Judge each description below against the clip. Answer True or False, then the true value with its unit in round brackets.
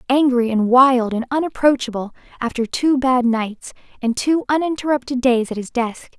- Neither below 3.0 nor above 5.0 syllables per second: True (4.9 syllables/s)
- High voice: True (255 Hz)